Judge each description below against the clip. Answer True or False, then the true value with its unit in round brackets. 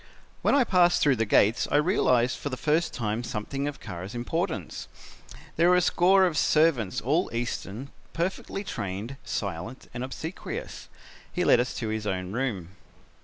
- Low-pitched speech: True (125 Hz)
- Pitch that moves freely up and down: True (7.1 semitones)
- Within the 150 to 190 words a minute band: True (165 wpm)